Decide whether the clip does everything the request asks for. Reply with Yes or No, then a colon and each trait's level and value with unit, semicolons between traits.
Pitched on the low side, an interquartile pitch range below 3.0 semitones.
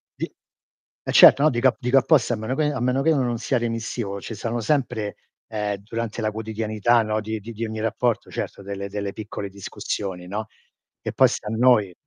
Yes: low, 110 Hz; narrow, 2.6 semitones